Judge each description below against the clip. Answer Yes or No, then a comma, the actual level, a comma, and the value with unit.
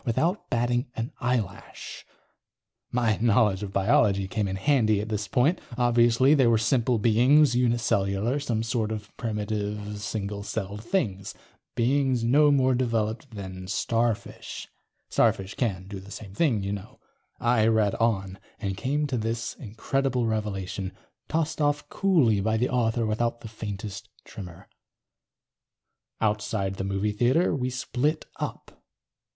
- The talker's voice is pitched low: Yes, low, 115 Hz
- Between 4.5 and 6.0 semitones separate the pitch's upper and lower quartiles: No, average, 3.5 semitones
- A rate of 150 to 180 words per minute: No, average, 140 wpm